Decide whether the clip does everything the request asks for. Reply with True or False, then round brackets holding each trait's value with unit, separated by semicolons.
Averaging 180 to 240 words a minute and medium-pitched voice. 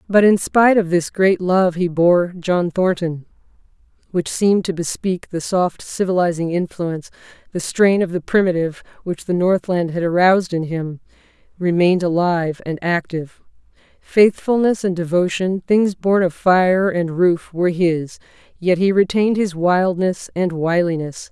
False (150 wpm; 180 Hz)